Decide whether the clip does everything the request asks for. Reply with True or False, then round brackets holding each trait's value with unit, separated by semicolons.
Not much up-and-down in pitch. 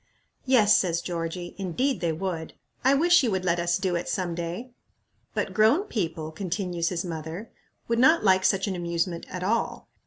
False (4.2 semitones)